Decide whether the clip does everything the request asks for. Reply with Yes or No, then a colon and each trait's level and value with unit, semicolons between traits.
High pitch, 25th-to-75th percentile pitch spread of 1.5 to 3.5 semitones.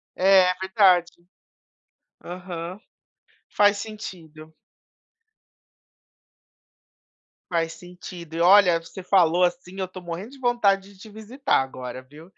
No: medium, 180 Hz; average, 2.9 semitones